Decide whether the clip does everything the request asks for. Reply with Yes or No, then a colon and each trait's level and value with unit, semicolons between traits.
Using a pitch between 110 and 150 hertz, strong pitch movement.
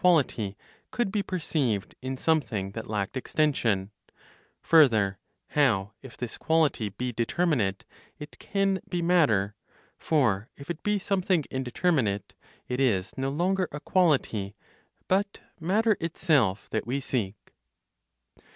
Yes: low, 135 Hz; wide, 8.0 semitones